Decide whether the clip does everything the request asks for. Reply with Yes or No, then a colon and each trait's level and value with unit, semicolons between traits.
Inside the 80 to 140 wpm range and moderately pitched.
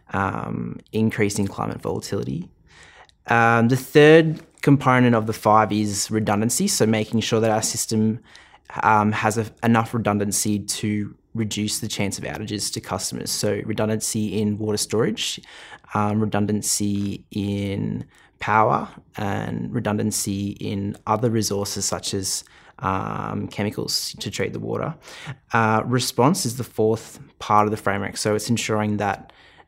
No: slow, 135 wpm; low, 110 Hz